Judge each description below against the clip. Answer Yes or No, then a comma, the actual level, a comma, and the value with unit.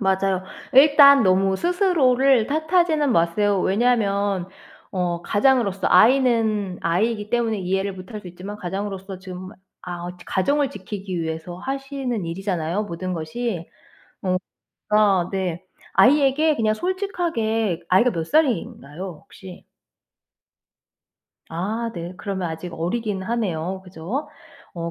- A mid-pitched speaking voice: No, high, 200 Hz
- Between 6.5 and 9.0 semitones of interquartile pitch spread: No, average, 5.2 semitones